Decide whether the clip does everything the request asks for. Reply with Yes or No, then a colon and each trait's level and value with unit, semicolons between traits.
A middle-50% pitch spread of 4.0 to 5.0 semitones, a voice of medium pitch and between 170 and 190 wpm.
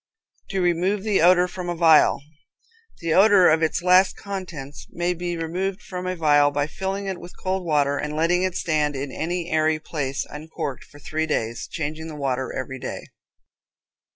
No: average, 3.5 semitones; medium, 165 Hz; average, 180 wpm